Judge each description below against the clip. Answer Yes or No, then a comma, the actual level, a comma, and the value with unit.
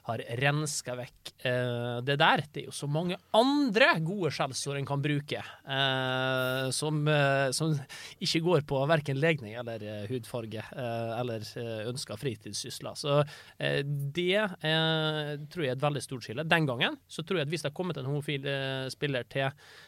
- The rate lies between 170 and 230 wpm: No, average, 150 wpm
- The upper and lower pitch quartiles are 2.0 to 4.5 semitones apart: Yes, average, 3.8 semitones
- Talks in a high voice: No, medium, 140 Hz